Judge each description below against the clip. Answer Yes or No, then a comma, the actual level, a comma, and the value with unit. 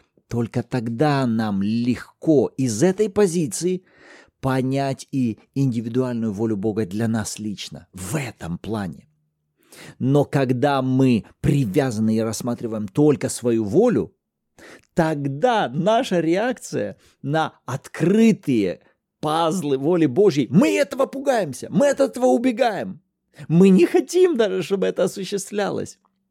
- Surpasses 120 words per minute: No, slow, 110 wpm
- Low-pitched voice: No, medium, 145 Hz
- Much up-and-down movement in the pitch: Yes, wide, 8.1 semitones